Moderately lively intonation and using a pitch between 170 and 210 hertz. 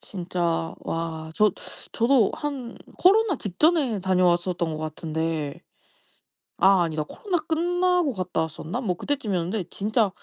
No: wide, 8.8 semitones; high, 190 Hz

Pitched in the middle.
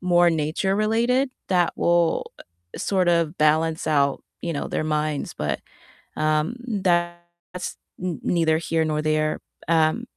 Yes: medium, 165 Hz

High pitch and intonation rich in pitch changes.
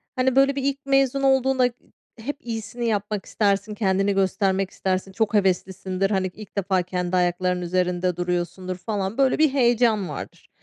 No: high, 200 Hz; average, 4.6 semitones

